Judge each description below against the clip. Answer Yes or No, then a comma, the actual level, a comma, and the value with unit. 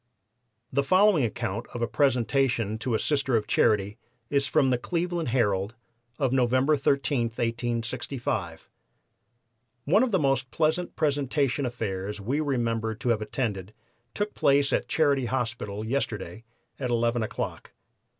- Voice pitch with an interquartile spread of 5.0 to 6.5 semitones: No, average, 4.0 semitones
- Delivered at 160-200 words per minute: No, slow, 135 wpm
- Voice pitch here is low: Yes, low, 125 Hz